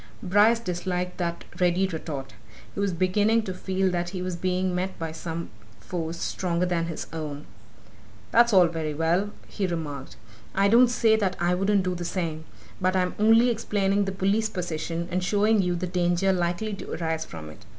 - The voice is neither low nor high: Yes, medium, 180 Hz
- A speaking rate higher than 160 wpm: Yes, average, 180 wpm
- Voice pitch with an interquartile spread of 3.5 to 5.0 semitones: No, narrow, 2.6 semitones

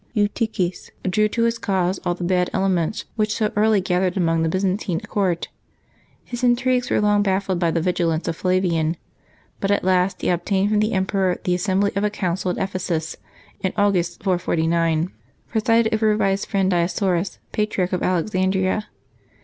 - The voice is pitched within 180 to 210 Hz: Yes, high, 190 Hz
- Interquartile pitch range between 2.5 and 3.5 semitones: Yes, average, 2.8 semitones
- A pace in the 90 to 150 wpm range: No, average, 165 wpm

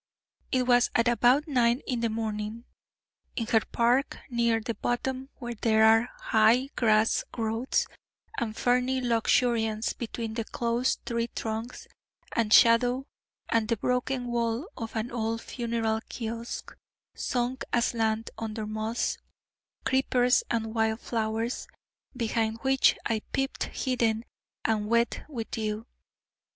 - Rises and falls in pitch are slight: Yes, narrow, 1.8 semitones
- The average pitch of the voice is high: Yes, high, 230 Hz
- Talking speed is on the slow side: Yes, slow, 125 wpm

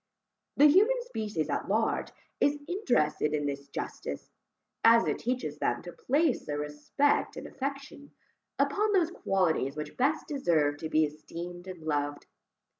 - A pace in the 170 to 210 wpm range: No, average, 145 wpm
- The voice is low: No, high, 190 Hz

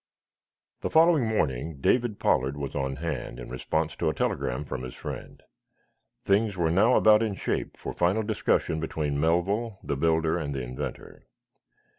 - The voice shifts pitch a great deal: Yes, wide, 6.9 semitones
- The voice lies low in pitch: Yes, very low, 80 Hz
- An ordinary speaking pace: Yes, average, 160 wpm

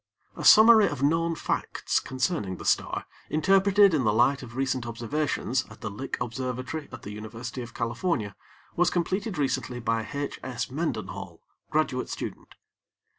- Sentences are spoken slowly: No, average, 150 wpm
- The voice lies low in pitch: Yes, low, 130 Hz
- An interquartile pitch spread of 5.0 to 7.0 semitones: Yes, wide, 5.5 semitones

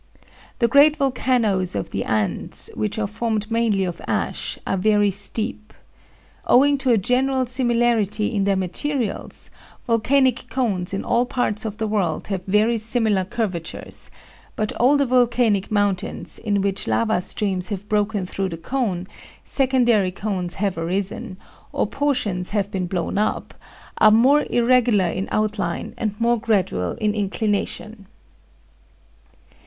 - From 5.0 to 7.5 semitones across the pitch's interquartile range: No, average, 3.8 semitones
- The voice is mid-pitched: No, high, 215 Hz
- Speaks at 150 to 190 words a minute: No, average, 140 wpm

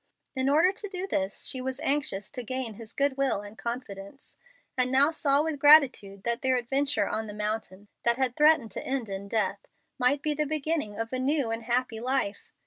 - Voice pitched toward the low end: No, very high, 255 Hz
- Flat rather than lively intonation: No, average, 4.4 semitones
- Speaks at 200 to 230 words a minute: Yes, fast, 205 wpm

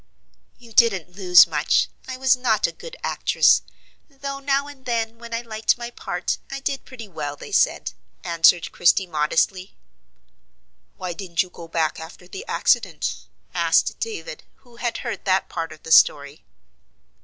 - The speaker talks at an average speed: Yes, average, 160 wpm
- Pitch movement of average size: No, wide, 6.9 semitones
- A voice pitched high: Yes, high, 200 Hz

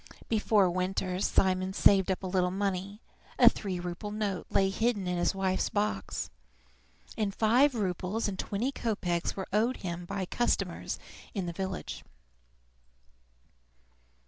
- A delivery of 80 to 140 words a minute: Yes, slow, 135 wpm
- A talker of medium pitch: No, high, 195 Hz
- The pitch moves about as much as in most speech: No, narrow, 2.3 semitones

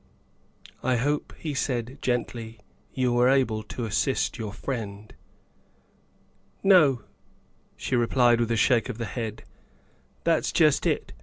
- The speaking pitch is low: Yes, low, 120 Hz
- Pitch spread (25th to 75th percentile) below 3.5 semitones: Yes, narrow, 2.6 semitones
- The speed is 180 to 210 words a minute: No, average, 145 wpm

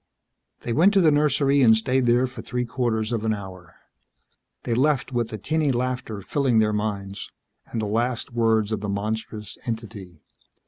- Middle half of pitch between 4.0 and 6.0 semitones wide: No, average, 3.1 semitones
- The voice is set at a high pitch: No, low, 115 Hz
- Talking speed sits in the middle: Yes, average, 175 wpm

